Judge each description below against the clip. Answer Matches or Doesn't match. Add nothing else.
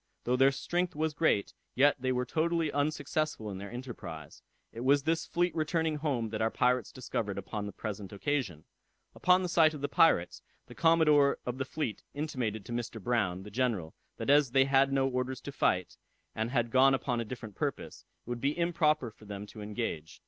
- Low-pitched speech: Matches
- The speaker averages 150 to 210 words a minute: Matches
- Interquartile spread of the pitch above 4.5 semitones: Matches